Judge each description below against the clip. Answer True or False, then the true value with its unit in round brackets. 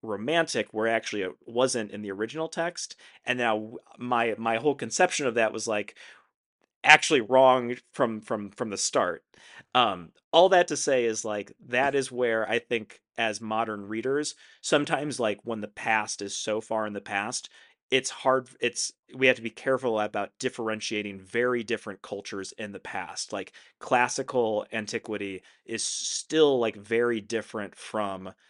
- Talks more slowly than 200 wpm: True (160 wpm)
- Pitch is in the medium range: False (115 Hz)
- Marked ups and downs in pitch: False (3.1 semitones)